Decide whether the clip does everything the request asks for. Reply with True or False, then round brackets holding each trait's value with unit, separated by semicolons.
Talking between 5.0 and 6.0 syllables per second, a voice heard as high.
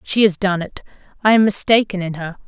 True (5.8 syllables/s; 195 Hz)